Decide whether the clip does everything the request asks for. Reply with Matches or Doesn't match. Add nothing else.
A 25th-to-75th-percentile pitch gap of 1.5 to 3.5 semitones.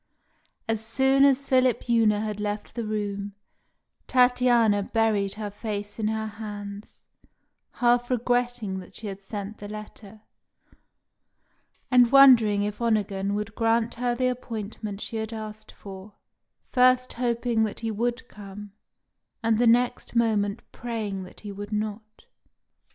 Matches